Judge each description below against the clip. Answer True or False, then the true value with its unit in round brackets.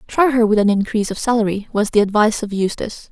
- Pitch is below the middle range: False (215 Hz)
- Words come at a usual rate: False (230 wpm)